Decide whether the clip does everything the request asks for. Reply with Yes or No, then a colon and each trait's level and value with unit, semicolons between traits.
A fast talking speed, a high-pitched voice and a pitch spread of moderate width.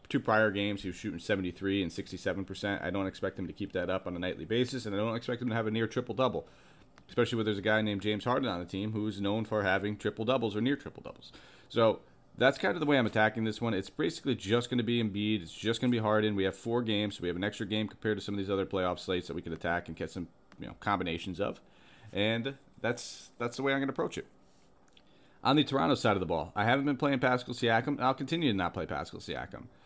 No: fast, 270 wpm; low, 110 Hz; average, 3.5 semitones